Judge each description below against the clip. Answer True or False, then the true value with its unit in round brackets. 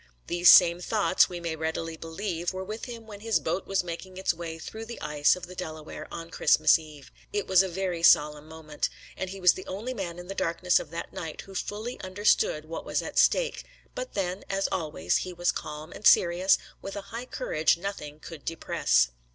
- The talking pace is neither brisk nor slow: False (210 wpm)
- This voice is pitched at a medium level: True (175 Hz)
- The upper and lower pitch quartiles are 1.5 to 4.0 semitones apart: True (3.3 semitones)